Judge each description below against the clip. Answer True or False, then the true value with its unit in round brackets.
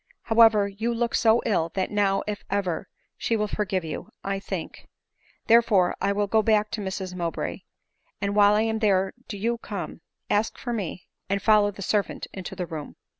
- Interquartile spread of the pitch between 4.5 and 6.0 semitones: False (2.4 semitones)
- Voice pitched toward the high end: True (205 Hz)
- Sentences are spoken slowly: False (185 wpm)